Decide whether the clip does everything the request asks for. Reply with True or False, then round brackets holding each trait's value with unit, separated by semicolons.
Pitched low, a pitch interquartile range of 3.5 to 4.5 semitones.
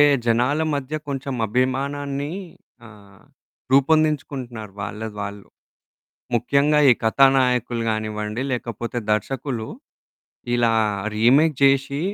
True (125 Hz; 3.9 semitones)